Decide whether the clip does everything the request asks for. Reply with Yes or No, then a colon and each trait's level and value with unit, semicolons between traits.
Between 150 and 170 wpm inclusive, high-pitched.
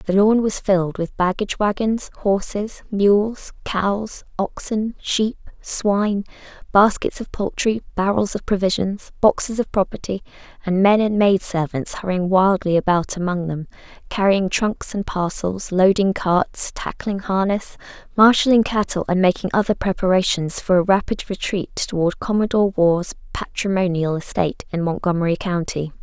No: slow, 135 wpm; high, 195 Hz